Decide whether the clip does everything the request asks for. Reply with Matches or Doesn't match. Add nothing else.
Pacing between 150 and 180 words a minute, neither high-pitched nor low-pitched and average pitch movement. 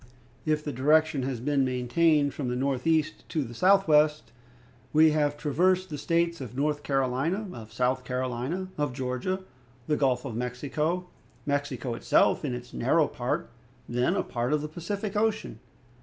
Matches